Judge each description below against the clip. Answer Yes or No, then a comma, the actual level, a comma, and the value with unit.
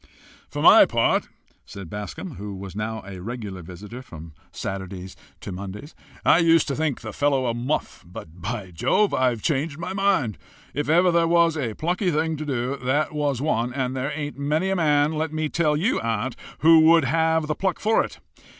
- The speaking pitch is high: No, medium, 140 Hz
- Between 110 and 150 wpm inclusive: No, average, 190 wpm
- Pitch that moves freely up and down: Yes, wide, 6.8 semitones